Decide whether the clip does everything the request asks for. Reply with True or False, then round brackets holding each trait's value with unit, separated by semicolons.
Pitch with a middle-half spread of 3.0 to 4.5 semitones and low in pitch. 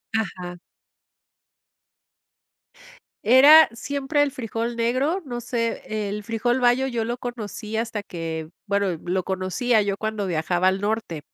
False (4.0 semitones; 225 Hz)